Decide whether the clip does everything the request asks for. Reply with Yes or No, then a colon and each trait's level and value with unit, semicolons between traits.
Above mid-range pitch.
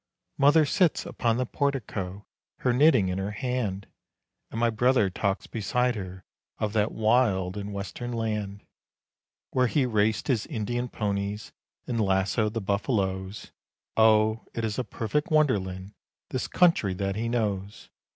No: low, 110 Hz